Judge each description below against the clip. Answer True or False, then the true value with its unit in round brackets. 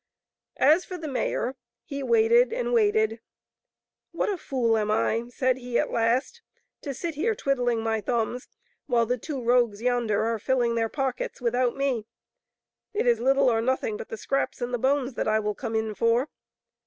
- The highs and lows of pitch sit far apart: False (3.3 semitones)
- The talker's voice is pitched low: False (245 Hz)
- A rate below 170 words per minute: False (190 wpm)